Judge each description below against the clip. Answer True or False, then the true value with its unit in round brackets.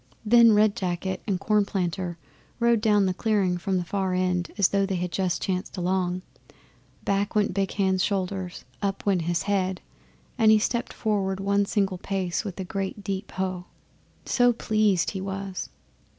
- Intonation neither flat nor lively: False (1.8 semitones)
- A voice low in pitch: False (195 Hz)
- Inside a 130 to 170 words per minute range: True (165 wpm)